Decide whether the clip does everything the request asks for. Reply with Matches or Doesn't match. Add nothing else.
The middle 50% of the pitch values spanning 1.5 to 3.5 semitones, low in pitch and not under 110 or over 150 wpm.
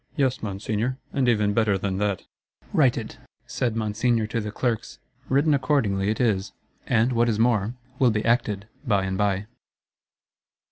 Matches